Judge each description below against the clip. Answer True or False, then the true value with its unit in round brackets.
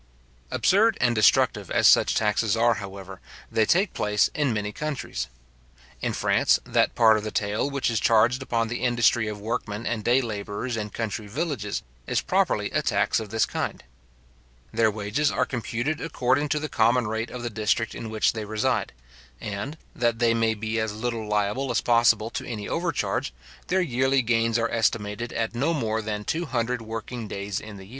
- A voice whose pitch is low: True (115 Hz)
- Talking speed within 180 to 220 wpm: True (185 wpm)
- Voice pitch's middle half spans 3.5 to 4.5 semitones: False (2.6 semitones)